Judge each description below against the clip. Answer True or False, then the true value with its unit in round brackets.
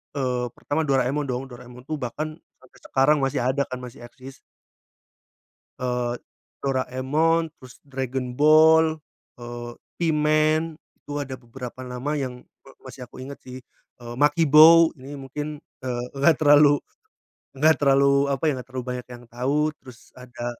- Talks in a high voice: False (135 Hz)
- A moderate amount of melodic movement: True (3.1 semitones)